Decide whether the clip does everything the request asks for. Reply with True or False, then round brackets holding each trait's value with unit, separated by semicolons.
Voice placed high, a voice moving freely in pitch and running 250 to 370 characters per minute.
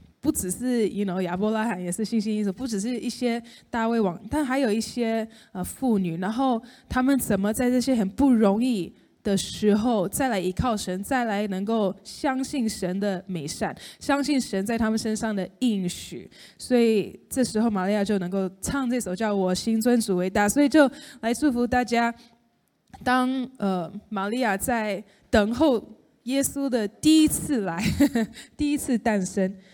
False (225 Hz; 3.9 semitones; 260 characters per minute)